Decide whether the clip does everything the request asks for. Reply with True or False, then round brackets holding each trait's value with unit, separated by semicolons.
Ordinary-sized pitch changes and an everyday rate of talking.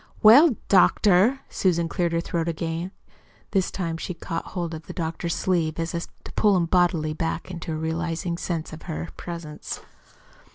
False (1.8 semitones; 170 wpm)